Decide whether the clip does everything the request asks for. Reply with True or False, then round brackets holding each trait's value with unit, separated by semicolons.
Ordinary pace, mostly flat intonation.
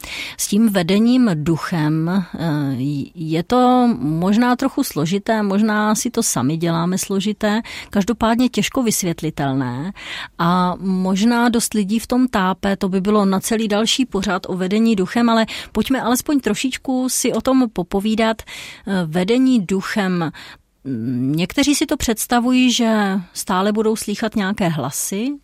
False (130 wpm; 4.5 semitones)